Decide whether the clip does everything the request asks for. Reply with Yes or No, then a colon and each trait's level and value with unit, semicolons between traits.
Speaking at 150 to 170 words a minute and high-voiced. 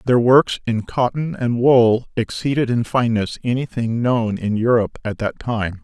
No: average, 165 wpm; low, 120 Hz